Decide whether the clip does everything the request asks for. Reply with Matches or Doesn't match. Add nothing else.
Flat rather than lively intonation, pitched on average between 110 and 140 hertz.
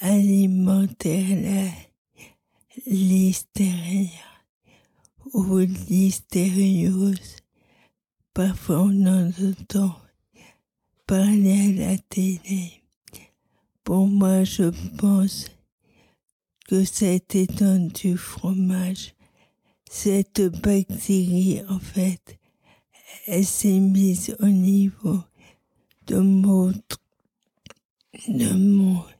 Doesn't match